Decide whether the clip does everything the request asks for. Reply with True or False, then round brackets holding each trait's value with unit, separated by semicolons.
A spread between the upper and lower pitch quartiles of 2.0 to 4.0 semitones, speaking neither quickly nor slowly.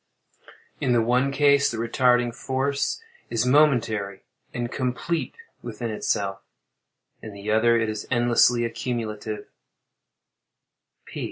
False (2.7 semitones; 100 wpm)